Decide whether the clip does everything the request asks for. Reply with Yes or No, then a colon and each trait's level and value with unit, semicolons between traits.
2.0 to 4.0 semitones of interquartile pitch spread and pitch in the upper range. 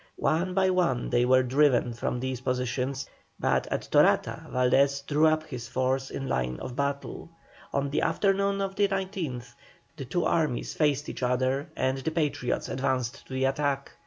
No: average, 3.6 semitones; low, 135 Hz